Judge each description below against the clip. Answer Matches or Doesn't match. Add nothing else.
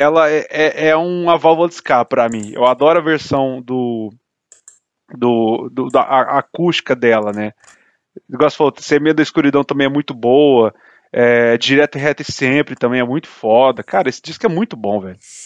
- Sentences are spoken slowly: Doesn't match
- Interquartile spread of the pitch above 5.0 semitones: Doesn't match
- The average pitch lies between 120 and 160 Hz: Matches